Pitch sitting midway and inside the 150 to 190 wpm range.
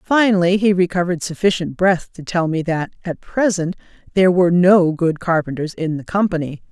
Yes: medium, 175 Hz; average, 170 wpm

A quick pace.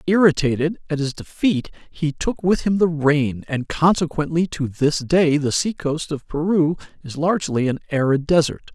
No: average, 170 wpm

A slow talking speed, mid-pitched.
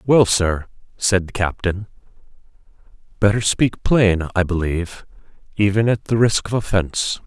No: slow, 130 wpm; low, 100 Hz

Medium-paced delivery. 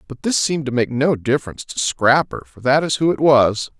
No: fast, 235 wpm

